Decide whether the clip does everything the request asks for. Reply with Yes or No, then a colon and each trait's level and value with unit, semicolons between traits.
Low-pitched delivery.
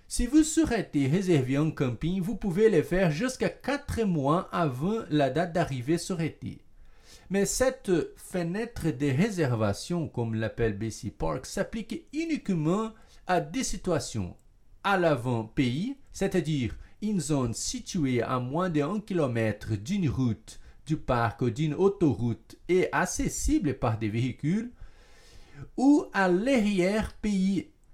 No: medium, 170 Hz